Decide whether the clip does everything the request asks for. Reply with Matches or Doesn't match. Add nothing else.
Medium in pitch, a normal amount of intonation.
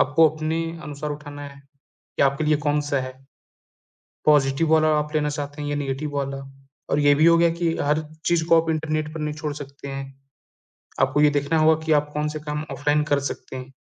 Doesn't match